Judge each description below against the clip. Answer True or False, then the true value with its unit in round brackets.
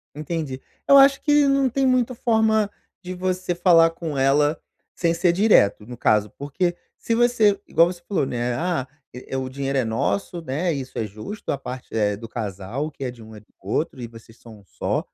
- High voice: False (150 Hz)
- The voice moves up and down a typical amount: False (7.9 semitones)